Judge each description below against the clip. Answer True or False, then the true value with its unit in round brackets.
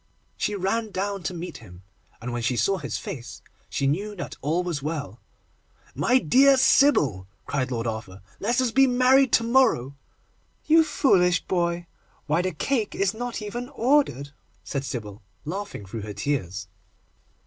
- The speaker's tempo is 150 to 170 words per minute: True (160 wpm)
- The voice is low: False (180 Hz)